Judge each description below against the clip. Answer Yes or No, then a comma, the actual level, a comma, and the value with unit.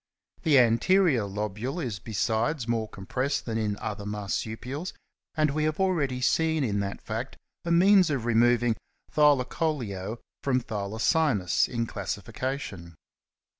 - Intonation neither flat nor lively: No, wide, 5.8 semitones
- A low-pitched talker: Yes, low, 120 Hz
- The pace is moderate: No, slow, 130 wpm